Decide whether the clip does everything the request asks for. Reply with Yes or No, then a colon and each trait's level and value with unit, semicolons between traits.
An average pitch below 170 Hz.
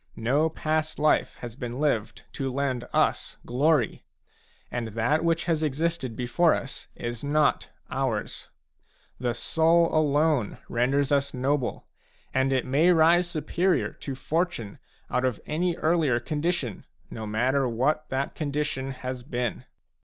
Yes: medium, 140 Hz